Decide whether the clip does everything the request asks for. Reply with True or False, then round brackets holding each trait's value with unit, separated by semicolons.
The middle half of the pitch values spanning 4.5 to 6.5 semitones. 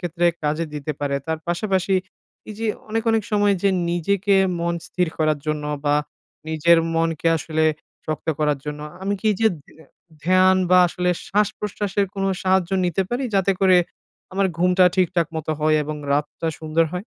False (3.7 semitones)